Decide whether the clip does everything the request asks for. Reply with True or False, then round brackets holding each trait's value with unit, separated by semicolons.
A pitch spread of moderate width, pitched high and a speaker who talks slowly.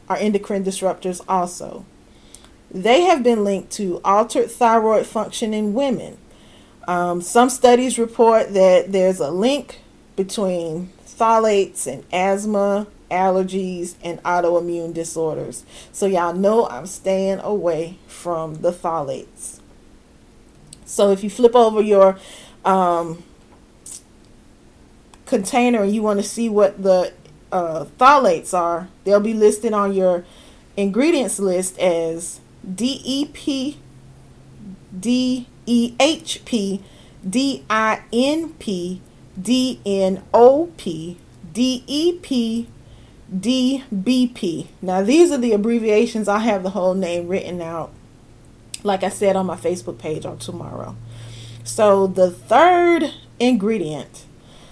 True (4.8 semitones; 195 Hz; 120 wpm)